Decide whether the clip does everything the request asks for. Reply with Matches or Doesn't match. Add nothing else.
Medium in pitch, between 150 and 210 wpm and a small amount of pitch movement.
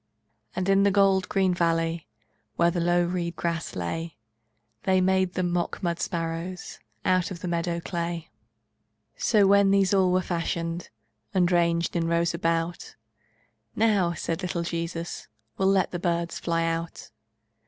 Matches